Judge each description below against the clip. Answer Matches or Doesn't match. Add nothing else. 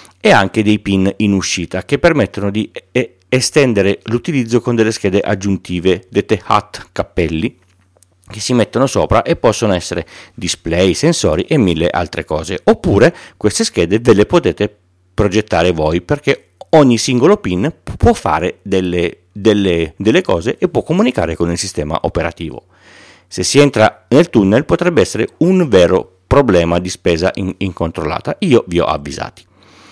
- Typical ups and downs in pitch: Matches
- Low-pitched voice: Matches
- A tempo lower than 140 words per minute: Doesn't match